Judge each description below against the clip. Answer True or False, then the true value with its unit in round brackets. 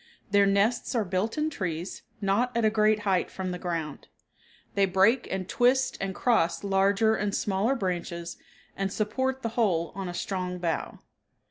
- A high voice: True (195 Hz)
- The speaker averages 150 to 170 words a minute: True (165 wpm)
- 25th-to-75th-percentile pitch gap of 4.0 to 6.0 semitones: False (3.4 semitones)